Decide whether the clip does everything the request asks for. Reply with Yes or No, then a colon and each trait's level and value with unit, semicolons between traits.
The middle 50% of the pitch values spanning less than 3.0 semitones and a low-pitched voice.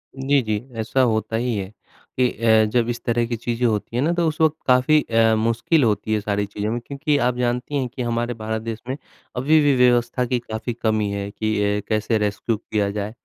Yes: narrow, 2.6 semitones; low, 120 Hz